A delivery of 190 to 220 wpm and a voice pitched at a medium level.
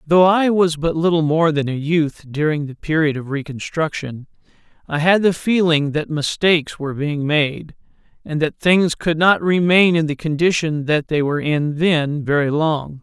No: average, 180 wpm; medium, 155 Hz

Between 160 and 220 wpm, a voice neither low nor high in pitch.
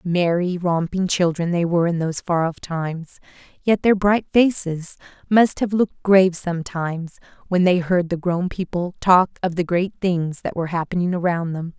Yes: average, 180 wpm; medium, 175 Hz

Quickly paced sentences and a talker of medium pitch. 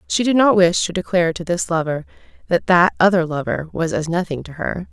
Yes: fast, 220 wpm; medium, 175 Hz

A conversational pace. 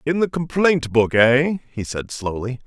Yes: average, 180 wpm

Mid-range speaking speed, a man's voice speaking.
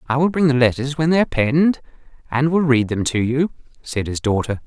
No: fast, 230 wpm; male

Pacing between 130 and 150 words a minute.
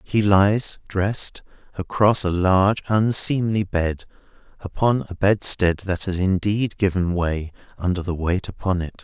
Yes: average, 140 wpm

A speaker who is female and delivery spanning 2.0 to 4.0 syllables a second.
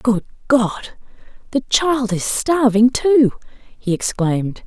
Yes: female; 3.4 syllables/s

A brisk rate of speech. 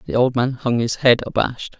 Yes: fast, 235 wpm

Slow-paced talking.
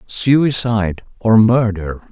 Yes: slow, 115 wpm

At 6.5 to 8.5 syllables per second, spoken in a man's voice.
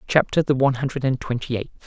Yes: 7.0 syllables/s; male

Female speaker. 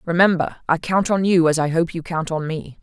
Yes: female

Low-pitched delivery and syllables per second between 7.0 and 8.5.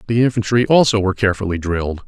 Yes: low, 105 Hz; 7.5 syllables/s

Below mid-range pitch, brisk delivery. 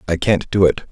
Yes: very low, 90 Hz; fast, 265 wpm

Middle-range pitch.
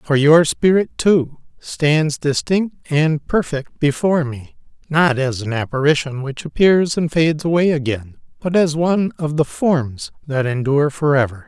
Yes: medium, 150 Hz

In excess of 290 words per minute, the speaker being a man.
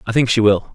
Yes: fast, 320 wpm; male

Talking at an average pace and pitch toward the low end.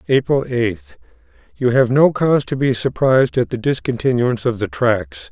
Yes: average, 160 wpm; low, 125 Hz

